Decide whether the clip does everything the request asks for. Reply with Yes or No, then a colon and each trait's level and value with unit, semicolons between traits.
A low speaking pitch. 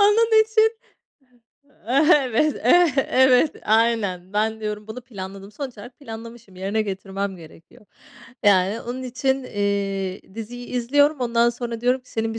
No: high, 230 Hz